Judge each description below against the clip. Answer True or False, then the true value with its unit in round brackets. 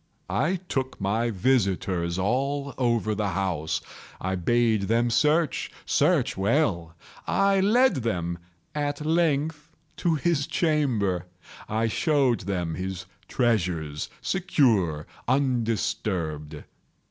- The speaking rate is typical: False (100 wpm)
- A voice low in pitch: True (115 Hz)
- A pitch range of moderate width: False (7.6 semitones)